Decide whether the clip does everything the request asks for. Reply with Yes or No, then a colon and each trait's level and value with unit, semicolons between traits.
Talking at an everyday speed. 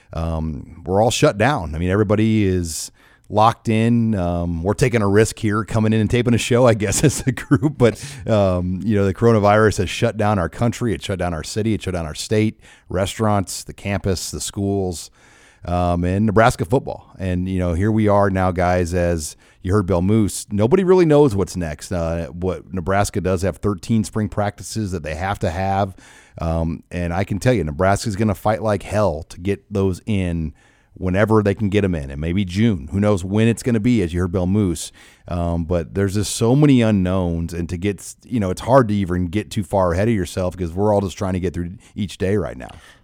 No: fast, 225 wpm